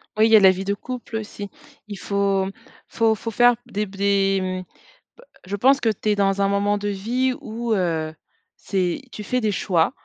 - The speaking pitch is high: Yes, high, 205 Hz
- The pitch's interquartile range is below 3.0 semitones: Yes, narrow, 2.4 semitones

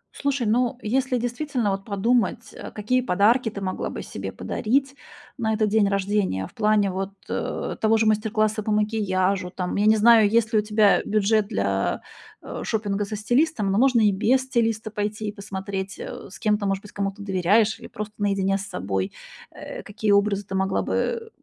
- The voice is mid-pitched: No, high, 210 Hz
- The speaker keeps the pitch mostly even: Yes, narrow, 2.2 semitones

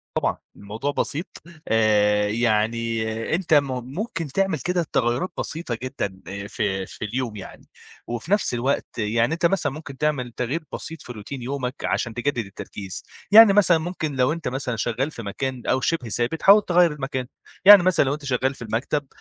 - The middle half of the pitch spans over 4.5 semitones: Yes, wide, 5.6 semitones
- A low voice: Yes, low, 130 Hz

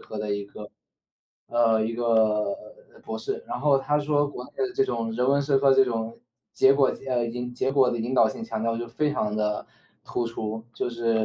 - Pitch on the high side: No, low, 120 Hz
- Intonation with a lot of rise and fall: No, average, 3.4 semitones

